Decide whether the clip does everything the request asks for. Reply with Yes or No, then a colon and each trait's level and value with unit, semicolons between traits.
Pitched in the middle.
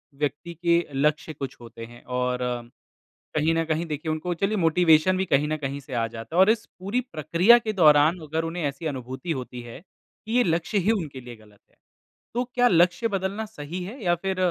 Yes: medium, 160 Hz